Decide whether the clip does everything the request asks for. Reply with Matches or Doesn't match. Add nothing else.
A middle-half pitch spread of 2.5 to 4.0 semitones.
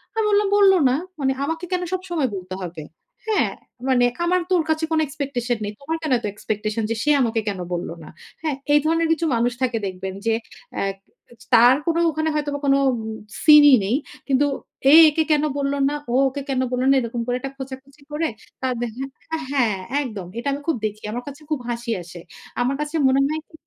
Doesn't match